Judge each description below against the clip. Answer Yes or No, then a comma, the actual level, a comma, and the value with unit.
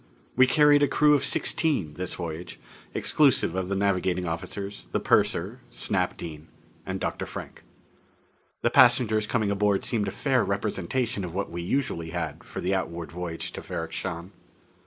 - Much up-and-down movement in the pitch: Yes, wide, 5.9 semitones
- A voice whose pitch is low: Yes, low, 100 Hz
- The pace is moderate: Yes, average, 160 wpm